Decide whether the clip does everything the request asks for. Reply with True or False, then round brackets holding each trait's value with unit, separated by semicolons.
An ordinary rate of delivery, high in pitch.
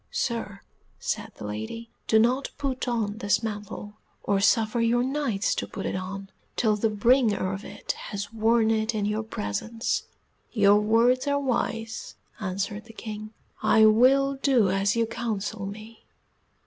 True (155 wpm; 220 Hz)